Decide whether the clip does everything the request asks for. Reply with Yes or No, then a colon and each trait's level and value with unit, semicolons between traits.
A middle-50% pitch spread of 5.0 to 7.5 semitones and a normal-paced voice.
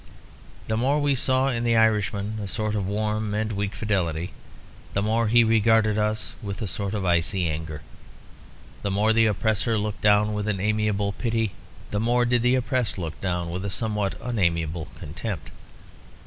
No: narrow, 2.4 semitones; average, 175 wpm